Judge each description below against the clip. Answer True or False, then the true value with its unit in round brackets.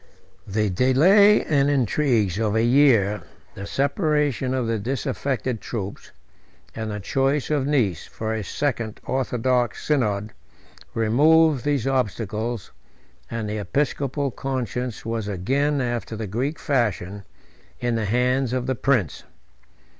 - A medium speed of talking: False (125 wpm)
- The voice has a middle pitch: False (125 Hz)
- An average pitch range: True (4.2 semitones)